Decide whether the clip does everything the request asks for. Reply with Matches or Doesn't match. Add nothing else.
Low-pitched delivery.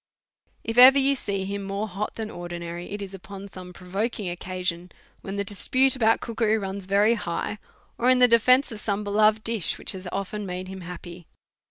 Doesn't match